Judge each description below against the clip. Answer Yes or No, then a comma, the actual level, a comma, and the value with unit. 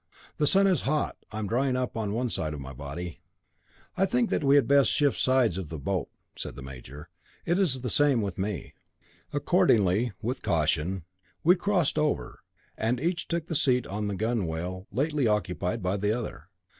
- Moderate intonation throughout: No, wide, 7.9 semitones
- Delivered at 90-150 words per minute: No, average, 190 wpm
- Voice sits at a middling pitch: No, low, 115 Hz